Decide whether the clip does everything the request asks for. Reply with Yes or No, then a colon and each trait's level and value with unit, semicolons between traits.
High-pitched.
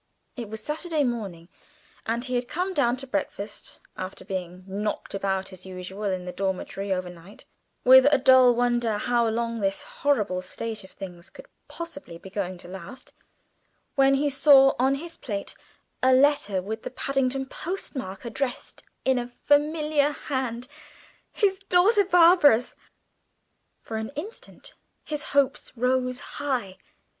Yes: high, 245 Hz